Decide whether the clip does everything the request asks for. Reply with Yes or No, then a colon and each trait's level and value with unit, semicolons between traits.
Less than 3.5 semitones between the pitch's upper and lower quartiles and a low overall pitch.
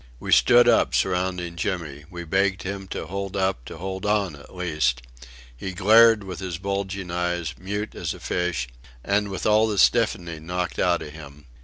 Yes: narrow, 2.6 semitones; very low, 95 Hz